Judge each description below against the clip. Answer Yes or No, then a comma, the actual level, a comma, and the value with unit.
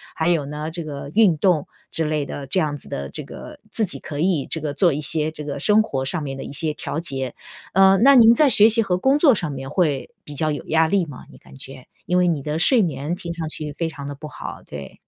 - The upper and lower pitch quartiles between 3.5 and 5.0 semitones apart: Yes, average, 4.0 semitones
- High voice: No, medium, 155 Hz